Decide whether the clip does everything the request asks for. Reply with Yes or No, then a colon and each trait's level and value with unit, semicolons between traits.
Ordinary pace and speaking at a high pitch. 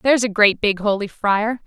No: fast, 215 wpm; high, 215 Hz